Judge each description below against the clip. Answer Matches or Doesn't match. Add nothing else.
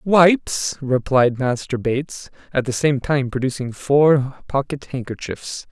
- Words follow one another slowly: Matches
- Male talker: Matches